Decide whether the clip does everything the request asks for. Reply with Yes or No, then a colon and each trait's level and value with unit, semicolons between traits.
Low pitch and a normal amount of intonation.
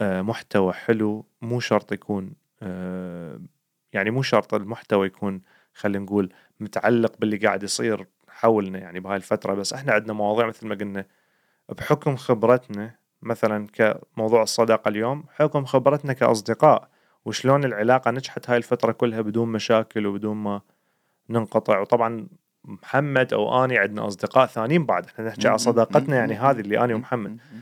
Yes: low, 110 Hz; average, 3.2 semitones